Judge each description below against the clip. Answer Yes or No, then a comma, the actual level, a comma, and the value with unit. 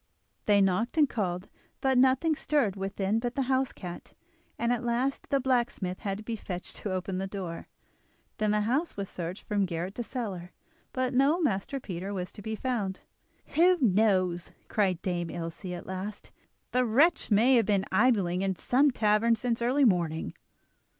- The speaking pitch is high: Yes, high, 210 Hz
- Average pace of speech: Yes, average, 175 wpm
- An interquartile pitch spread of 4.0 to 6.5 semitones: Yes, average, 5.1 semitones